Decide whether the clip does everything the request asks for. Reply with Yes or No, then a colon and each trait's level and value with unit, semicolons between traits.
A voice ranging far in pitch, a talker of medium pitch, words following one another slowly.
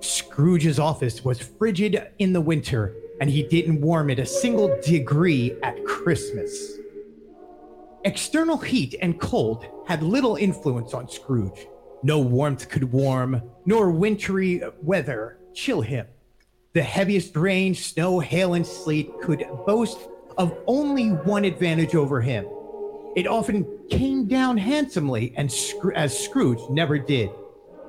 Yes: wide, 7.4 semitones; medium, 175 Hz; slow, 130 wpm